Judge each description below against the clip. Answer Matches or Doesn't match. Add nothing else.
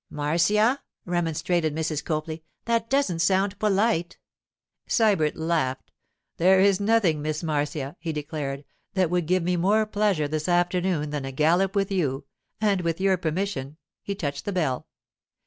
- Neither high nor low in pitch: Matches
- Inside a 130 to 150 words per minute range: Matches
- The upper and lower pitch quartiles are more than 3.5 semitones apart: Matches